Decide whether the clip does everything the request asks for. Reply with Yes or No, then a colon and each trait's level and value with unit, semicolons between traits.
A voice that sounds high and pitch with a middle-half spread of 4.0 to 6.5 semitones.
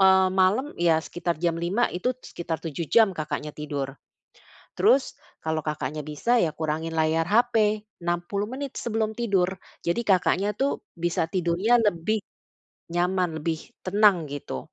No: medium, 175 Hz; average, 4.7 semitones